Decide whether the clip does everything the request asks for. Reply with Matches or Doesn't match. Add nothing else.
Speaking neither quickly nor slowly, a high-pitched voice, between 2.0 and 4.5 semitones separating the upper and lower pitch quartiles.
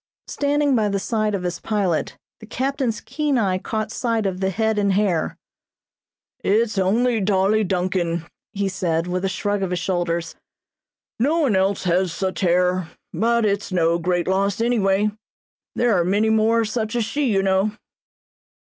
Matches